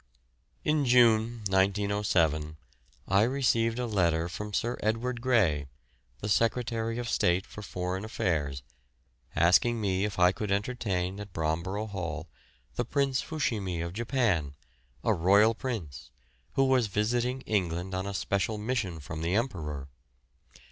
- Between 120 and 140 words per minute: Yes, slow, 135 wpm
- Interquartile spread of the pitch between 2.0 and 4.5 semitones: No, average, 4.9 semitones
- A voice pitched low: Yes, low, 100 Hz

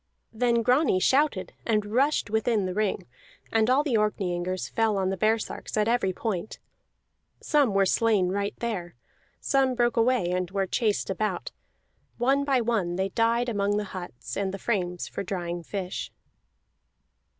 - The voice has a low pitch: No, high, 210 Hz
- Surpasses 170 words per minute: No, average, 155 wpm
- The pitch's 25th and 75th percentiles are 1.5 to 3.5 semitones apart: No, average, 4.1 semitones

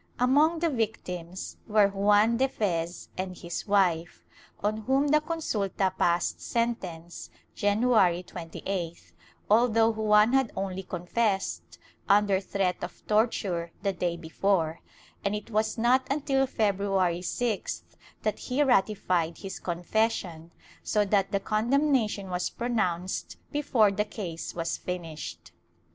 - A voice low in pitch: No, high, 200 Hz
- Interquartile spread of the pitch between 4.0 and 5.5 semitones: Yes, average, 4.3 semitones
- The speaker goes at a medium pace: No, slow, 125 wpm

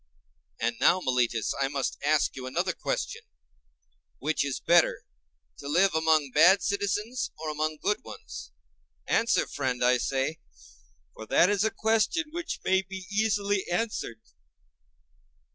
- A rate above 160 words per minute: No, slow, 135 wpm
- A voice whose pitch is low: No, medium, 160 Hz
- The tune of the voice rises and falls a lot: Yes, wide, 6.9 semitones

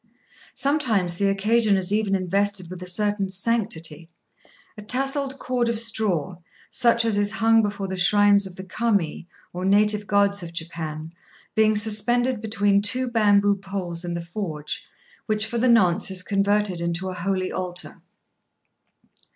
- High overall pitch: Yes, high, 200 Hz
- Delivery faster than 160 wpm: No, average, 150 wpm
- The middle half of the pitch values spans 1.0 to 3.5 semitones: Yes, average, 3.2 semitones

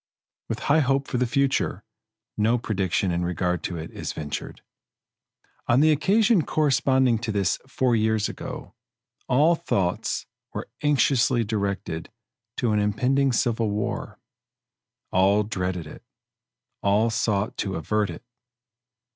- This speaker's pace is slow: Yes, slow, 130 wpm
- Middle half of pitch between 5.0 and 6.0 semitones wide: Yes, average, 5.3 semitones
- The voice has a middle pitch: No, low, 110 Hz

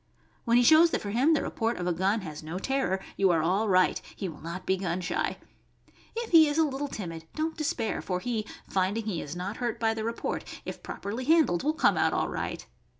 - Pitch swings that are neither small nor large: No, wide, 6.7 semitones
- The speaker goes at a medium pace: No, fast, 235 wpm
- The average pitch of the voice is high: Yes, high, 215 Hz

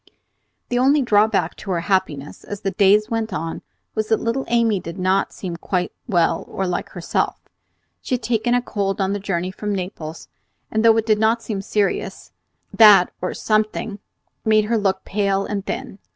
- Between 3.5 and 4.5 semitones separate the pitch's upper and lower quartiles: No, average, 2.7 semitones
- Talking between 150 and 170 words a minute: No, average, 180 wpm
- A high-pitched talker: Yes, high, 205 Hz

